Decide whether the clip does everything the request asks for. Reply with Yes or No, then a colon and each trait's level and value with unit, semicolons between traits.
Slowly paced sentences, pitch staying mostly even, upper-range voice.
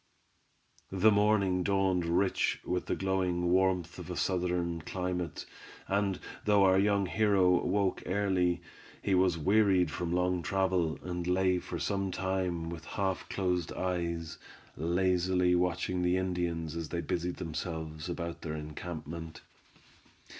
No: slow, 130 wpm; narrow, 1.7 semitones; very low, 90 Hz